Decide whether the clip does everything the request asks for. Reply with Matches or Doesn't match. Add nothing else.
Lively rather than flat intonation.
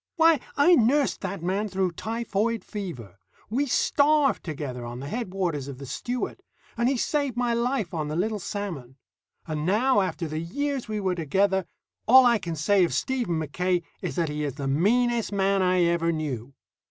Matches